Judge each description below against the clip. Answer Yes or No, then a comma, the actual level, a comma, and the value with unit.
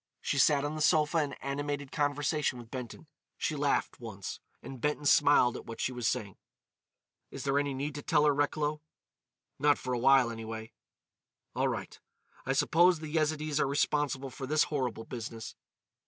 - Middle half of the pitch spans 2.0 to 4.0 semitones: Yes, average, 2.9 semitones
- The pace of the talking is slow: No, average, 170 wpm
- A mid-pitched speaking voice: Yes, medium, 145 Hz